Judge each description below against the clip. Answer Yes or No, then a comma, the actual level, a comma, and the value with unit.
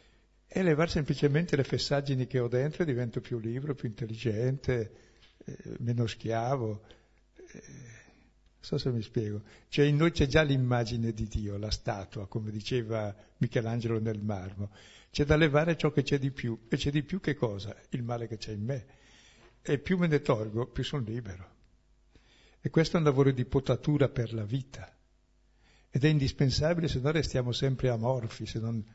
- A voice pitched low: Yes, low, 125 Hz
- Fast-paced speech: Yes, fast, 175 wpm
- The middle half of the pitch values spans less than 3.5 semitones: No, average, 4.4 semitones